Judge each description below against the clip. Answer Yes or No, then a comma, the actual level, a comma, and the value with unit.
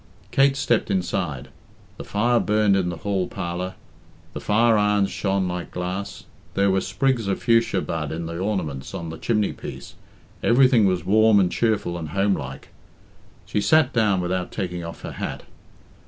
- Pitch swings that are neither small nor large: Yes, average, 3.4 semitones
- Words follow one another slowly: No, average, 160 wpm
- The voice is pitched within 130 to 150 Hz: No, very low, 95 Hz